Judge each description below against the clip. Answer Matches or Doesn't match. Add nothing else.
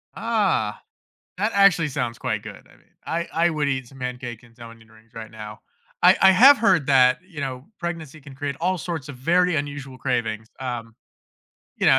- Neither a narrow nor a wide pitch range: Doesn't match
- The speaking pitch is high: Doesn't match